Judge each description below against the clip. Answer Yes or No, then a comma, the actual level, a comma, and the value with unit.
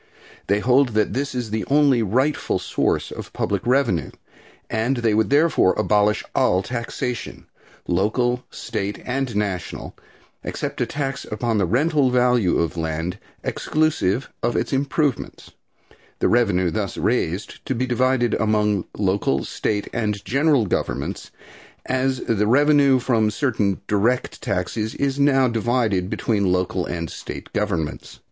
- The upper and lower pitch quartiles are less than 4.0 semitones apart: No, average, 4.4 semitones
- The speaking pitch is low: Yes, low, 115 Hz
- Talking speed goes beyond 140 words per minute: No, slow, 135 wpm